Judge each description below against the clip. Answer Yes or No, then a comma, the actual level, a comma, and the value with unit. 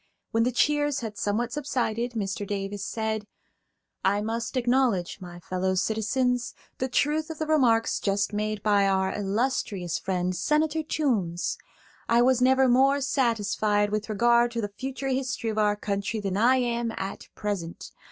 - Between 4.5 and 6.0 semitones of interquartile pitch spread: No, average, 4.1 semitones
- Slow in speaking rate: No, average, 155 wpm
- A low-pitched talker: No, high, 225 Hz